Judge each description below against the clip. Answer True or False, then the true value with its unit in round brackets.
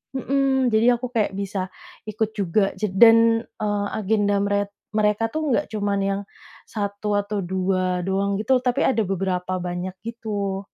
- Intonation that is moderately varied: False (2.2 semitones)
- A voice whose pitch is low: False (205 Hz)